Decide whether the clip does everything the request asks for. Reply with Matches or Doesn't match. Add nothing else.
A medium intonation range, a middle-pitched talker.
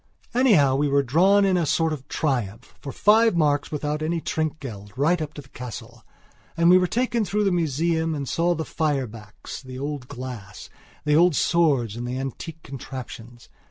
Matches